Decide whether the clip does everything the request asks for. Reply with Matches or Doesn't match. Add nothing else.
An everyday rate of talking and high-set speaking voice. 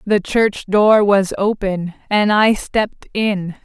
Matches